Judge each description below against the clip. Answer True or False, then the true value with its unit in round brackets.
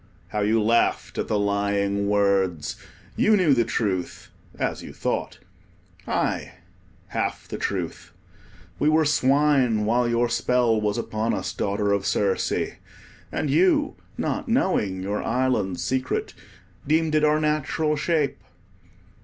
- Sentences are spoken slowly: True (130 wpm)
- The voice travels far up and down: True (6.7 semitones)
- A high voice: False (115 Hz)